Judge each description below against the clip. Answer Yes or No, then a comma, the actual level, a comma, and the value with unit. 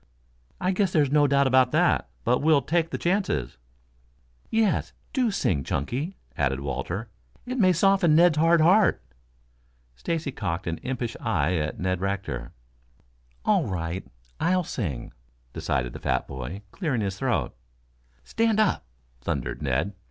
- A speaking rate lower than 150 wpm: Yes, average, 140 wpm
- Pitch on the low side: Yes, low, 125 Hz